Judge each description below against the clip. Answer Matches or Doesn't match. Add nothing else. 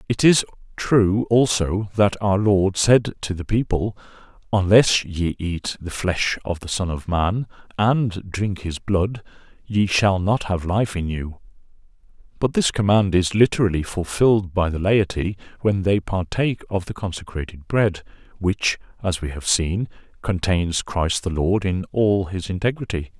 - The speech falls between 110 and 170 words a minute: Matches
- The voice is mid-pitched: Doesn't match